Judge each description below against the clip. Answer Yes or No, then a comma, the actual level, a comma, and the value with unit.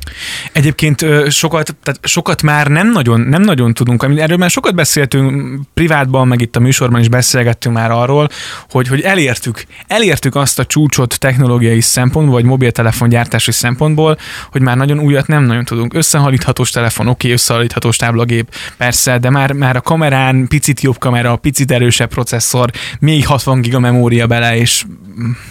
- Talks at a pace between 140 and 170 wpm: Yes, fast, 155 wpm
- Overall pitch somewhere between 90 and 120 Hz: No, low, 130 Hz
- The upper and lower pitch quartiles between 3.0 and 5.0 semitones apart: Yes, average, 3.5 semitones